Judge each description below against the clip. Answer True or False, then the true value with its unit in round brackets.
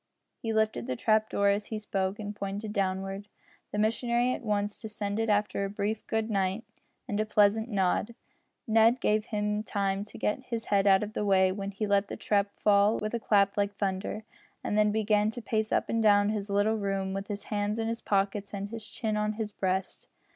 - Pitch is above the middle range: True (210 Hz)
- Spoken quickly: True (210 wpm)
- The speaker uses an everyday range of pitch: False (1.5 semitones)